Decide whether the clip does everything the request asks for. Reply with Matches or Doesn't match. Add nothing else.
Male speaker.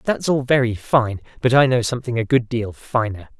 Matches